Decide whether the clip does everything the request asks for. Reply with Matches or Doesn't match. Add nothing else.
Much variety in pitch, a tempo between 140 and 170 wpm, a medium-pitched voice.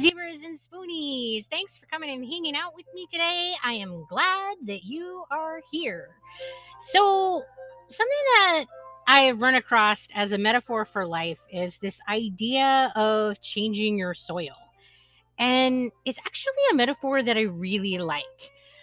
Doesn't match